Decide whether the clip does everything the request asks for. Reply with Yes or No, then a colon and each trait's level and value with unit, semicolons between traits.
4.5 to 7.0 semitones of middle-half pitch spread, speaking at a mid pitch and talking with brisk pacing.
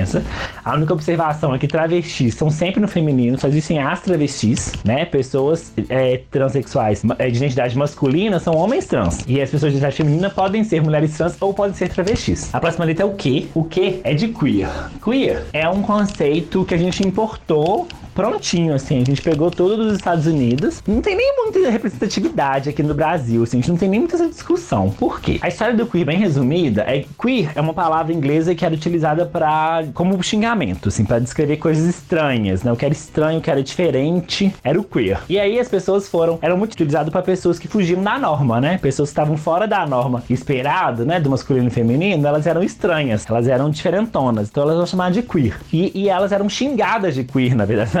Yes: average, 5.1 semitones; medium, 160 Hz; fast, 215 wpm